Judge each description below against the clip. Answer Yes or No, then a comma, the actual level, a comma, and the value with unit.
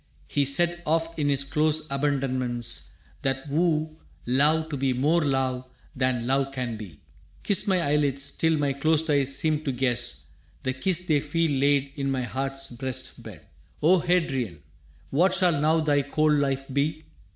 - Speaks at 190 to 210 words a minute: No, average, 165 wpm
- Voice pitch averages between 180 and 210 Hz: No, medium, 140 Hz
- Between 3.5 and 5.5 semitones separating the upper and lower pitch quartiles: No, average, 2.8 semitones